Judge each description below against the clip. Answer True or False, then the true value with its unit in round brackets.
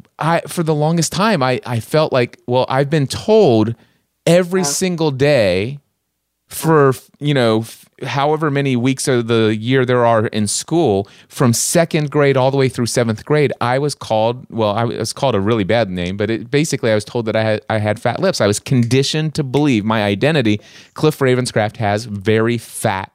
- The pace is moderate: True (195 wpm)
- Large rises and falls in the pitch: False (5.0 semitones)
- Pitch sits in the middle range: False (125 Hz)